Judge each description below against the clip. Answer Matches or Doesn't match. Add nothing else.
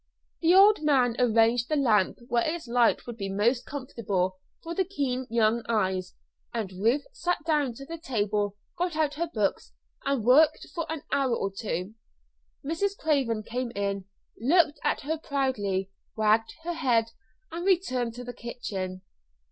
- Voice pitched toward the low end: Doesn't match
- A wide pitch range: Matches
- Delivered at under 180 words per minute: Matches